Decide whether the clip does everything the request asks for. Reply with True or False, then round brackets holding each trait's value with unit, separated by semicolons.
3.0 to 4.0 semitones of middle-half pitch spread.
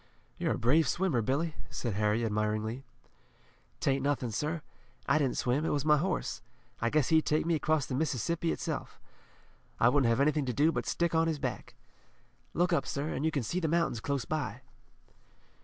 False (4.5 semitones)